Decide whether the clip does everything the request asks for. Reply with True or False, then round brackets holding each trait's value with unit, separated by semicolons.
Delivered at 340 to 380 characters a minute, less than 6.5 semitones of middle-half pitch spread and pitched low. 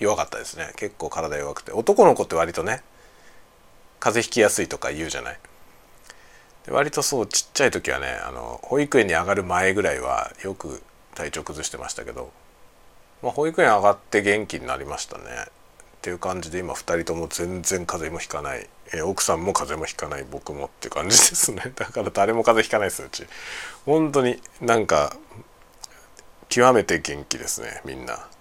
True (360 characters per minute; 5.4 semitones; 100 Hz)